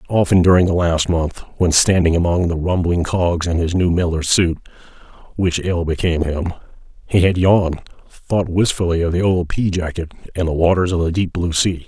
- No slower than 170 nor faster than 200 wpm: Yes, average, 190 wpm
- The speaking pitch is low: Yes, very low, 85 Hz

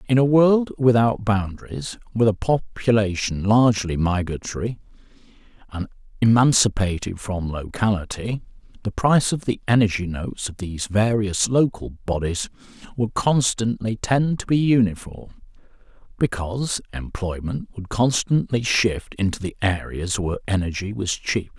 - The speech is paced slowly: Yes, slow, 120 wpm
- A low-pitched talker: Yes, low, 105 Hz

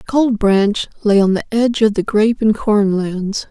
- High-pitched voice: Yes, high, 210 Hz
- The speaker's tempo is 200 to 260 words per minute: Yes, fast, 205 wpm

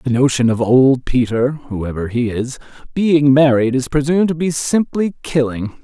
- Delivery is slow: No, average, 165 wpm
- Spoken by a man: Yes, male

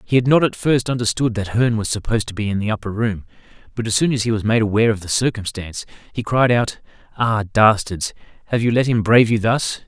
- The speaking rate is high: Yes, fast, 230 wpm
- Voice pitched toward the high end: No, low, 110 Hz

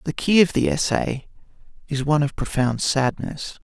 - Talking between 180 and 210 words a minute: No, average, 165 wpm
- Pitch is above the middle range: No, medium, 140 Hz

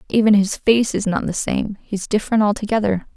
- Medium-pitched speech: No, high, 210 Hz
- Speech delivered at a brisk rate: No, average, 190 wpm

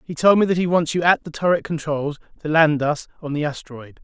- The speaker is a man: Yes, male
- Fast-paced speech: Yes, fast, 255 wpm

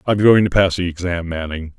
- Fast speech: Yes, fast, 235 wpm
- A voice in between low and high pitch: No, very low, 90 Hz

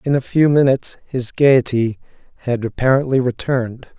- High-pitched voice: No, low, 130 Hz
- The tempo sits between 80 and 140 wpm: Yes, slow, 135 wpm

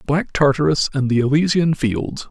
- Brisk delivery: No, average, 155 wpm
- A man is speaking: Yes, male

